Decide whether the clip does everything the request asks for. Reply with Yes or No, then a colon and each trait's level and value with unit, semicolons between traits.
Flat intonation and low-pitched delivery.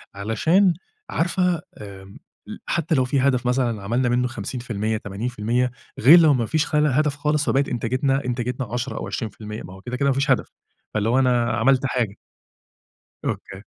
No: average, 3.6 semitones; low, 125 Hz